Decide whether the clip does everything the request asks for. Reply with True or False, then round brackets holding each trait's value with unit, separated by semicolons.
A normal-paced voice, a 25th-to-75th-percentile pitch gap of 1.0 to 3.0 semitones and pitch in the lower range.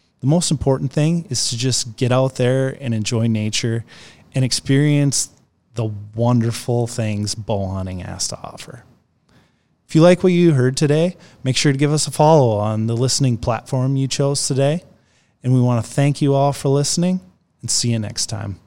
False (185 wpm; 3.9 semitones; 130 Hz)